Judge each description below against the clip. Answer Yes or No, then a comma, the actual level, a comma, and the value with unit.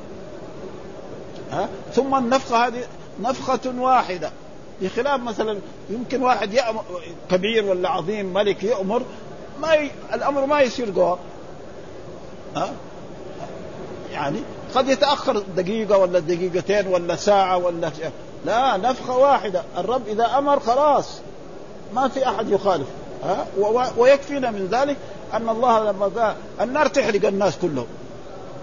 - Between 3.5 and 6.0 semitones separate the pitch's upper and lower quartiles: Yes, wide, 5.4 semitones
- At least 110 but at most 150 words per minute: Yes, average, 125 wpm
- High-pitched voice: Yes, high, 220 Hz